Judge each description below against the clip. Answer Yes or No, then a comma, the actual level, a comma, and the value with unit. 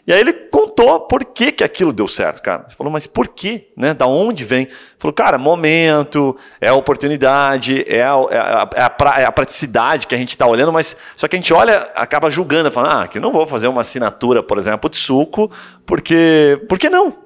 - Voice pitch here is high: No, medium, 155 Hz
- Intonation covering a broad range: Yes, wide, 7.3 semitones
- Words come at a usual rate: No, fast, 230 wpm